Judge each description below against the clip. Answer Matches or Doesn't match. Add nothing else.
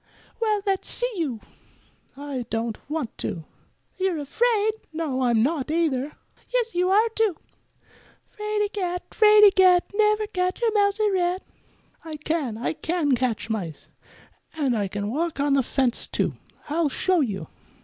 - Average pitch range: Doesn't match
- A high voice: Matches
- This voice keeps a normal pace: Matches